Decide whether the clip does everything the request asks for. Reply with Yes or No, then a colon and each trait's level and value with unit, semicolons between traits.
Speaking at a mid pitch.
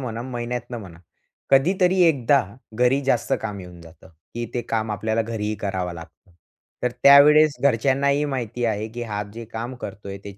No: low, 120 Hz